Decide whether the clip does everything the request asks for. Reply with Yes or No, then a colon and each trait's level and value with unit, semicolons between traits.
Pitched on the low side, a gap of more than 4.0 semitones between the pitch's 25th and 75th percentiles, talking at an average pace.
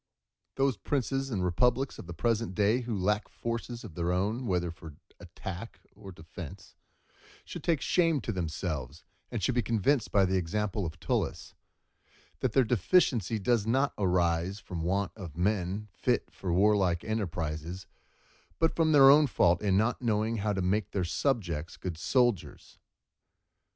Yes: low, 100 Hz; average, 5.0 semitones; average, 155 wpm